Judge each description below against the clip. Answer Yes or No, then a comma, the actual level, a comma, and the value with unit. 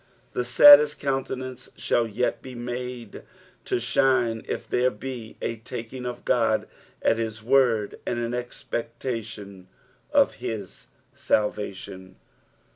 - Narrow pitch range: Yes, narrow, 2.3 semitones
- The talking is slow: Yes, slow, 120 wpm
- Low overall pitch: Yes, low, 120 Hz